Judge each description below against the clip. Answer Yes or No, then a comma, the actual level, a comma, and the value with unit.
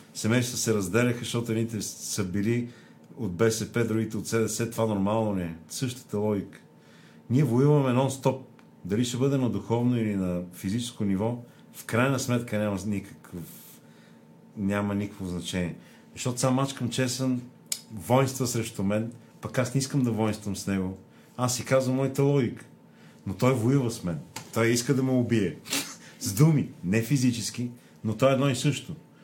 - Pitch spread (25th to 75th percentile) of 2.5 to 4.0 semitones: Yes, average, 3.7 semitones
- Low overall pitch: Yes, low, 115 Hz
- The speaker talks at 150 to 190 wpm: Yes, average, 160 wpm